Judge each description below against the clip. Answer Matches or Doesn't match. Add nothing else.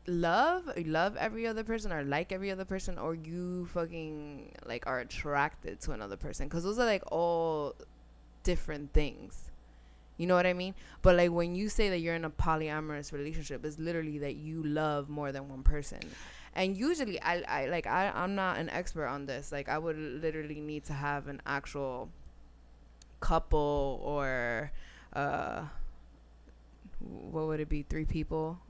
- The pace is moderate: Matches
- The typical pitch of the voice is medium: Matches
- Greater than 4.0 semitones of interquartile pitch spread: Doesn't match